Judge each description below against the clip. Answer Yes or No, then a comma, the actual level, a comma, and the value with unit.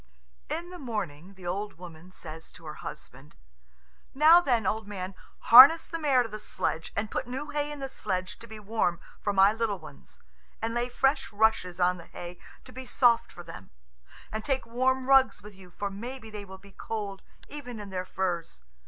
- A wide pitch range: Yes, wide, 5.7 semitones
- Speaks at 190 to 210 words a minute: Yes, average, 195 wpm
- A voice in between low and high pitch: No, high, 210 Hz